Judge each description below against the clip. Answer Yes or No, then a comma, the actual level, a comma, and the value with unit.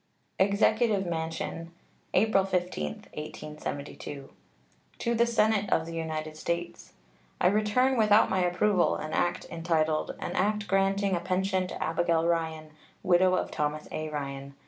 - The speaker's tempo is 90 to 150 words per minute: Yes, slow, 135 wpm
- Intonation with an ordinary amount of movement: Yes, average, 4.0 semitones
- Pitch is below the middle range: No, medium, 175 Hz